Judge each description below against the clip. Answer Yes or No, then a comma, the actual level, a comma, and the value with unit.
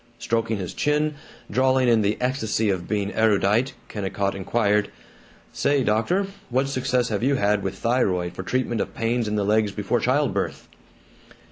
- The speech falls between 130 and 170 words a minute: Yes, average, 160 wpm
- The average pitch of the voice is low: Yes, low, 110 Hz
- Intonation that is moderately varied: Yes, average, 4.0 semitones